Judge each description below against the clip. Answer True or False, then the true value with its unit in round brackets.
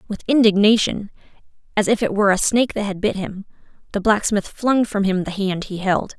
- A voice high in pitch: True (205 Hz)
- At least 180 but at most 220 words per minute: True (205 wpm)